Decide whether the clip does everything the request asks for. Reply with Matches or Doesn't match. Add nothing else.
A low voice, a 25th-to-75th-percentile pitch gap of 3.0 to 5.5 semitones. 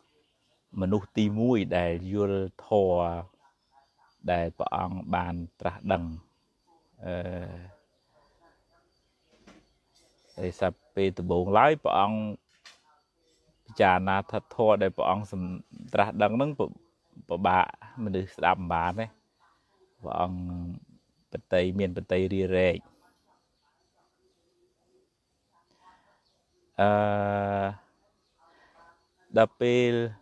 Doesn't match